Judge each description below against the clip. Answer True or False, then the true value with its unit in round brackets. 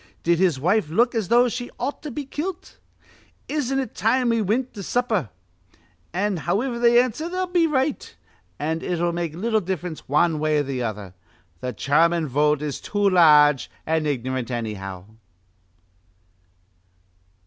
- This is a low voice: False (175 Hz)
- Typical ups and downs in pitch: False (8.3 semitones)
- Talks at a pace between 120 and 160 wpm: True (150 wpm)